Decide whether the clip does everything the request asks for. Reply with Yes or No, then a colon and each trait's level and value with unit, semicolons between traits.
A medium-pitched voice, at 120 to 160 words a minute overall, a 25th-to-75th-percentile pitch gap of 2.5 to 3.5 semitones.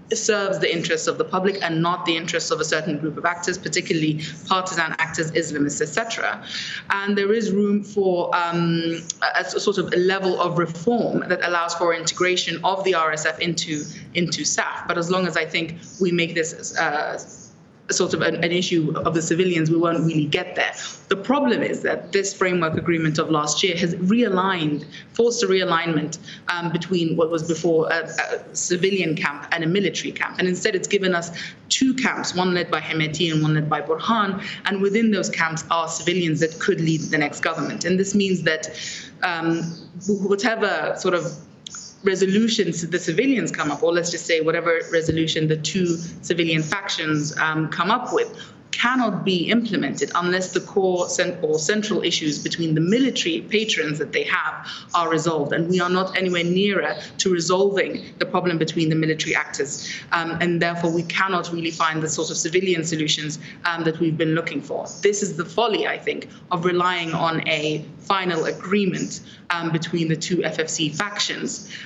No: medium, 175 Hz; average, 185 wpm; average, 2.8 semitones